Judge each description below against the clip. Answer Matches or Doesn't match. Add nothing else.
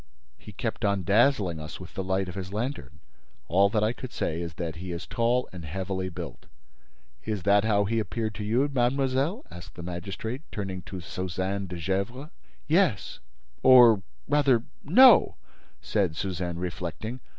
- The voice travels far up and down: Doesn't match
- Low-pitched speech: Matches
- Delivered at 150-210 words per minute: Matches